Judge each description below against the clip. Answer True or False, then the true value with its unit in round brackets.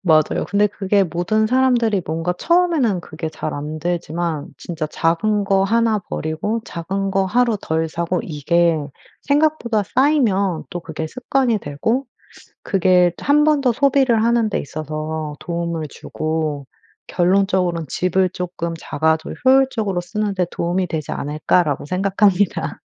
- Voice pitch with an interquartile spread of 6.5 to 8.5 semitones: False (5.2 semitones)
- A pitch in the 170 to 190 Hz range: True (185 Hz)